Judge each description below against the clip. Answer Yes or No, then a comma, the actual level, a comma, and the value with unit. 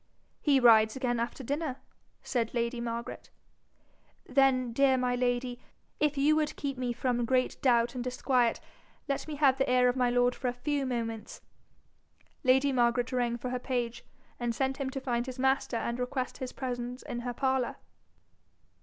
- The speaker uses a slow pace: No, average, 170 wpm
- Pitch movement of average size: No, narrow, 1.8 semitones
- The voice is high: Yes, very high, 250 Hz